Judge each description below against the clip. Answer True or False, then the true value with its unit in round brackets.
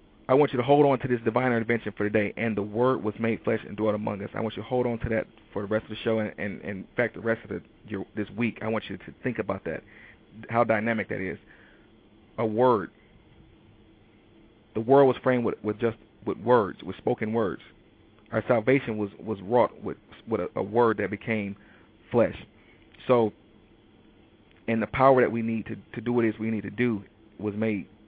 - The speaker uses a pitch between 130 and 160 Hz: False (110 Hz)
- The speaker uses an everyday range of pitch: False (1.7 semitones)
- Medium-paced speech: False (225 wpm)